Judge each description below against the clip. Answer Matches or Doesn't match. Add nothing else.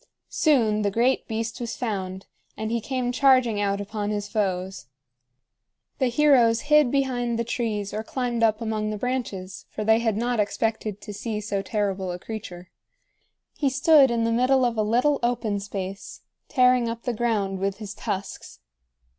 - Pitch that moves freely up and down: Doesn't match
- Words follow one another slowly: Doesn't match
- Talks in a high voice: Matches